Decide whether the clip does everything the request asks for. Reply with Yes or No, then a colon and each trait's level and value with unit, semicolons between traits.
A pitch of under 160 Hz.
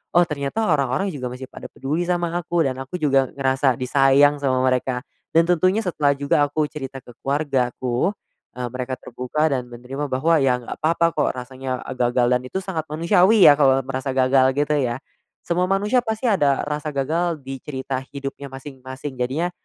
Yes: medium, 140 Hz